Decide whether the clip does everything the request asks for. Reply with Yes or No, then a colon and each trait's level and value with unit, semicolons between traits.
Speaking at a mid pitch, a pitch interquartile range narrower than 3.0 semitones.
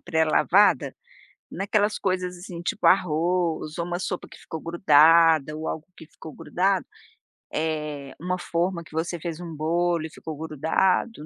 Yes: medium, 170 Hz; narrow, 2.4 semitones